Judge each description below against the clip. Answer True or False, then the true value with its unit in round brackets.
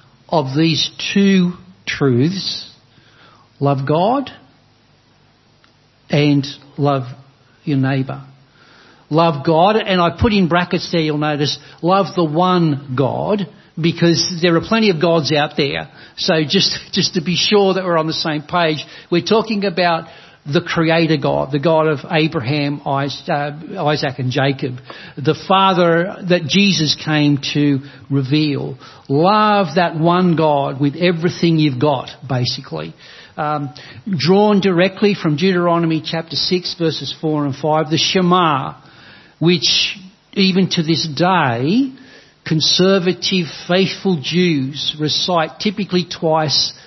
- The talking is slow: True (125 wpm)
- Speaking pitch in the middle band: True (160 Hz)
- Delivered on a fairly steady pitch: False (3.9 semitones)